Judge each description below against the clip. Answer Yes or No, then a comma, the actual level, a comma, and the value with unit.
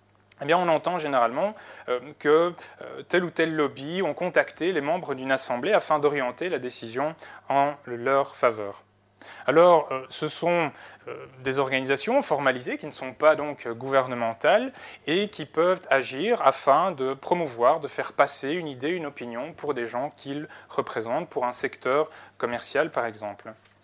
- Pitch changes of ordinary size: Yes, average, 3.3 semitones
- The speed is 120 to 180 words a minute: Yes, average, 150 wpm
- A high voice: No, medium, 140 Hz